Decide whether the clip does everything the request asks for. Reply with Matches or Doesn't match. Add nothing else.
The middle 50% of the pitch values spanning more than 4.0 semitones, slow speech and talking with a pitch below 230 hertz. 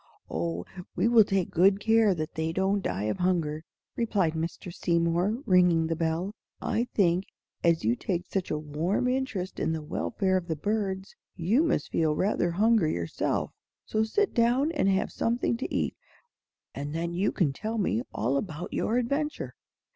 Doesn't match